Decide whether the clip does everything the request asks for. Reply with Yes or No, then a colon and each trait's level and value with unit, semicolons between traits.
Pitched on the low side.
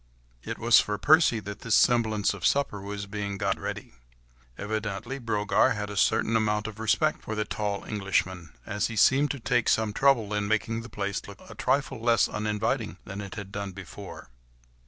Yes: low, 105 Hz